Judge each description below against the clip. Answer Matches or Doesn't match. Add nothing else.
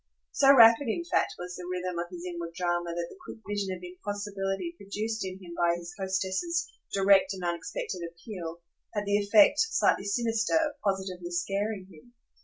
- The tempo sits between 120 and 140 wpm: Doesn't match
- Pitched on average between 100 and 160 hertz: Doesn't match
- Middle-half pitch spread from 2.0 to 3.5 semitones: Matches